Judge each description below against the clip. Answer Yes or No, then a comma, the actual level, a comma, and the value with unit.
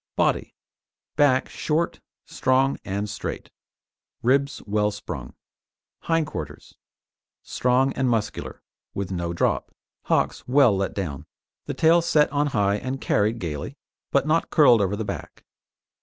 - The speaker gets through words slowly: Yes, slow, 130 wpm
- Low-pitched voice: Yes, low, 125 Hz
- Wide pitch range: Yes, wide, 5.9 semitones